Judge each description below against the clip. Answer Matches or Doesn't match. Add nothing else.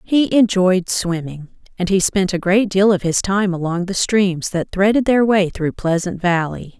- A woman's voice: Matches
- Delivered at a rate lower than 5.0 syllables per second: Matches